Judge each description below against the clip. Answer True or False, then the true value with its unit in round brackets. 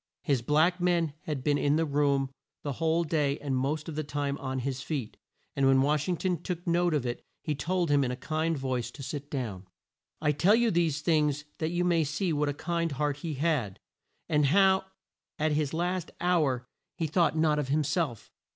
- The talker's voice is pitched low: False (150 Hz)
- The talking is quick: True (210 wpm)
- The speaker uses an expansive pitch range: False (3.1 semitones)